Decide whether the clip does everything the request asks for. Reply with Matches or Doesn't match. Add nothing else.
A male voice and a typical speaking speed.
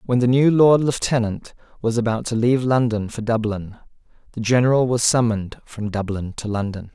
Matches